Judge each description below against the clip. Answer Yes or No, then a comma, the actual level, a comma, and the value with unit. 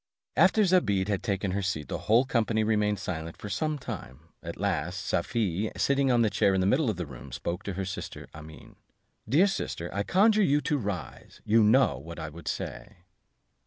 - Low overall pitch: Yes, low, 100 Hz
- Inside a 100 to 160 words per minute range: No, average, 200 wpm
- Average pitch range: No, wide, 5.9 semitones